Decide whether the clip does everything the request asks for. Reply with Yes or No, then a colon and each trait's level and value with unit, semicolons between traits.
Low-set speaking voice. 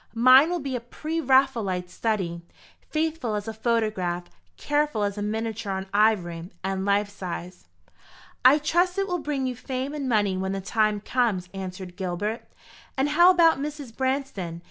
No: high, 225 Hz